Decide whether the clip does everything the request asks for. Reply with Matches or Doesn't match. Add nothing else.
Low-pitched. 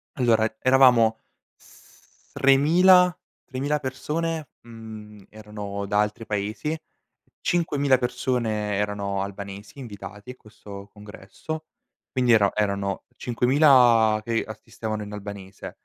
Matches